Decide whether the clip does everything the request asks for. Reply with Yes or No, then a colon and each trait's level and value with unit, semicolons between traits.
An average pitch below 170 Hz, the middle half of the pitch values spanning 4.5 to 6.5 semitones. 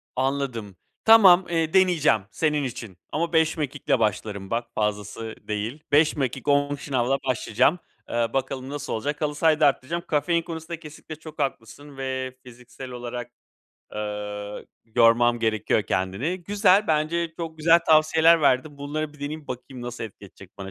Yes: medium, 140 Hz; average, 5.2 semitones